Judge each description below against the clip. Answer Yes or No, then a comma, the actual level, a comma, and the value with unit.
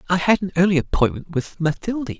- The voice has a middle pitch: Yes, medium, 175 Hz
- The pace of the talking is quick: No, average, 190 wpm